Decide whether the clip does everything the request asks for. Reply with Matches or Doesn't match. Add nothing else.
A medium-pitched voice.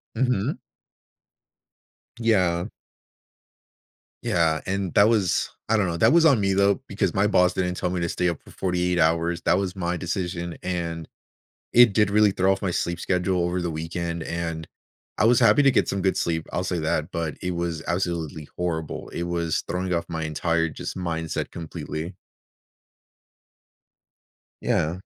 Doesn't match